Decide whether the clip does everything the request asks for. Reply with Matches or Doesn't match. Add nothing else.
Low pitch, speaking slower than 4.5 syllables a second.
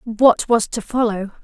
Doesn't match